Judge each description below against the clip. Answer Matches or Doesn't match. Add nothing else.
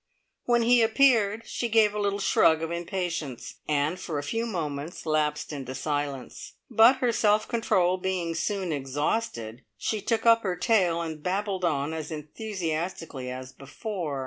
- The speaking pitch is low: Doesn't match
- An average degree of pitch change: Doesn't match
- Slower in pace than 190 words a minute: Matches